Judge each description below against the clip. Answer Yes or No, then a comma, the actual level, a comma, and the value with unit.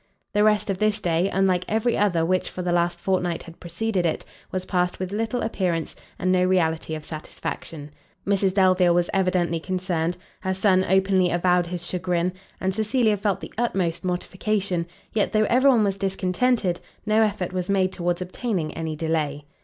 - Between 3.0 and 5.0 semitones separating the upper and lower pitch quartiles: No, narrow, 2.4 semitones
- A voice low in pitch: No, medium, 185 Hz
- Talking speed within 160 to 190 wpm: Yes, average, 175 wpm